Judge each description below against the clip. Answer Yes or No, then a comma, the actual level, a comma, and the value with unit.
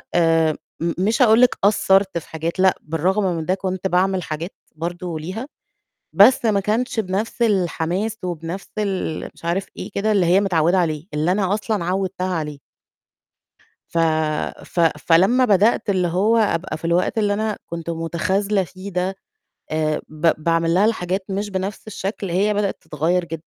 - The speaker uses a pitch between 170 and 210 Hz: Yes, medium, 185 Hz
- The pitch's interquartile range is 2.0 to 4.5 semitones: Yes, average, 3.3 semitones